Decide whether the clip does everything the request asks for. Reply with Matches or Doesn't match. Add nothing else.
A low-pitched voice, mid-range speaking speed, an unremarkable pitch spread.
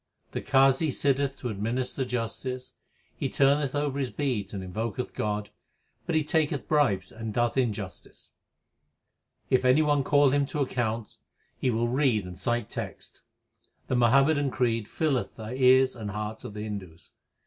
Matches